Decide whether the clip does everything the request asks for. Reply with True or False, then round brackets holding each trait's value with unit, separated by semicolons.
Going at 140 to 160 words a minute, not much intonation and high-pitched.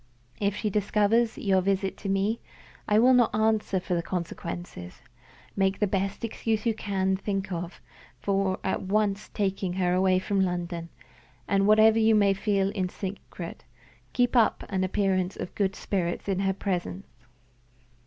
True (155 wpm; 2.1 semitones; 195 Hz)